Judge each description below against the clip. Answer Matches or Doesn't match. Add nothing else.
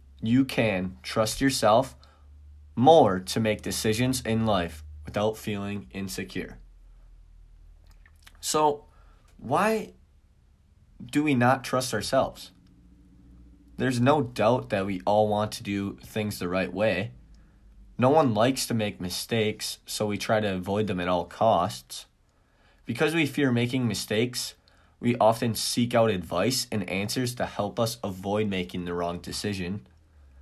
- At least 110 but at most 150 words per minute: Matches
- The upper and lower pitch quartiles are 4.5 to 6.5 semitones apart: Matches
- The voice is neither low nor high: Doesn't match